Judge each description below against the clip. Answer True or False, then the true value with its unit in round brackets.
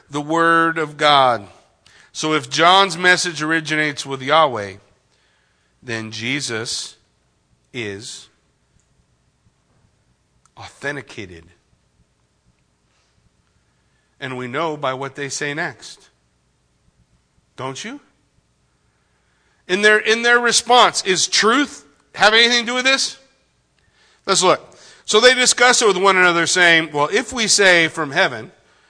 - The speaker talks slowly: True (110 wpm)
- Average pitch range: False (8.0 semitones)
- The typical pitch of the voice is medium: True (155 Hz)